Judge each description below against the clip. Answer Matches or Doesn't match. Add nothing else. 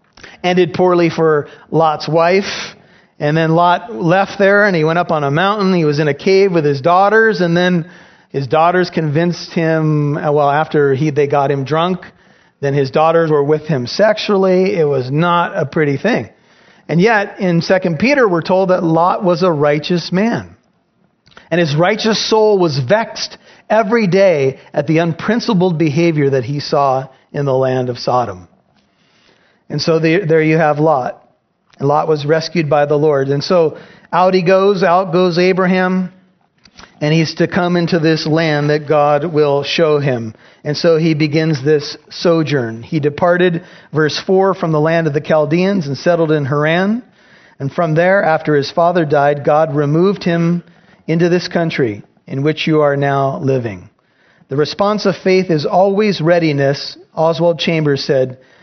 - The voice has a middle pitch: Matches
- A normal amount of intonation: Matches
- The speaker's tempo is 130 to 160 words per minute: Doesn't match